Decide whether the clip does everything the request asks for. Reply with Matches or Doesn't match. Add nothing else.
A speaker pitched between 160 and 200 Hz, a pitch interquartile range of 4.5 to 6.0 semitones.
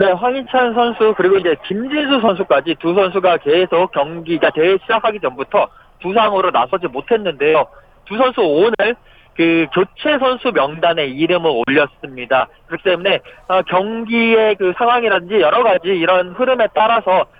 Matches